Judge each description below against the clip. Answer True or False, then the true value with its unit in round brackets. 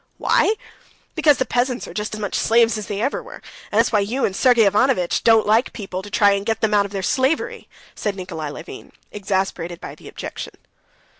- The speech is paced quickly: True (210 wpm)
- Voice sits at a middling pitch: False (210 Hz)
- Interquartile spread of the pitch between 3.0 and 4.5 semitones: True (3.3 semitones)